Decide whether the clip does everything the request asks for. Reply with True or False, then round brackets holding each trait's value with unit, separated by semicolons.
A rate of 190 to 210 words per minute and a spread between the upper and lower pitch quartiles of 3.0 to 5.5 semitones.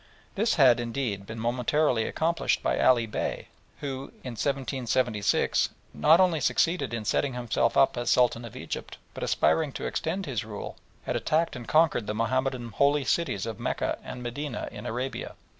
False (165 wpm; 3.8 semitones)